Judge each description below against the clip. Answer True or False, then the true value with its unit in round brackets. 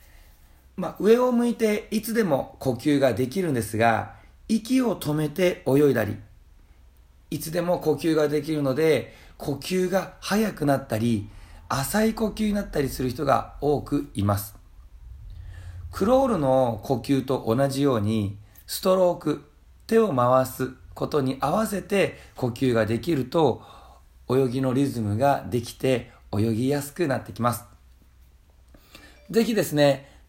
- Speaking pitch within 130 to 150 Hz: True (135 Hz)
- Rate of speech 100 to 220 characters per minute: False (260 characters per minute)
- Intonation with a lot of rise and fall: True (7.5 semitones)